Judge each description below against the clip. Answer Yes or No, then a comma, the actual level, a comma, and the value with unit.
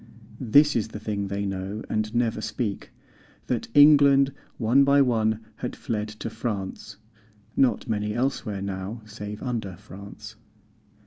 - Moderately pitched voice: No, low, 110 Hz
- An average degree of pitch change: Yes, average, 3.2 semitones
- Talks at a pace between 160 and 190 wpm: No, slow, 135 wpm